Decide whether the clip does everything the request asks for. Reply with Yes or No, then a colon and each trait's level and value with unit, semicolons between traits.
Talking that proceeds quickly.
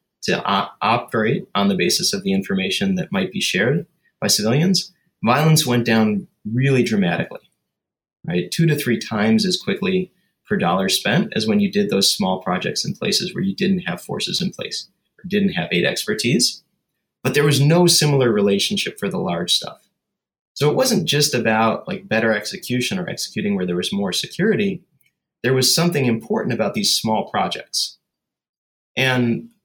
No: average, 170 wpm